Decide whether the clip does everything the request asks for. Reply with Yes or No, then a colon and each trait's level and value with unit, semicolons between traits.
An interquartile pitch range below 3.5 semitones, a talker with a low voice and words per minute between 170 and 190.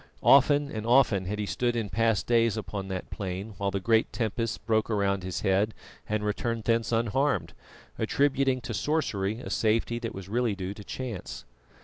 Yes: average, 3.1 semitones; low, 110 Hz; average, 175 wpm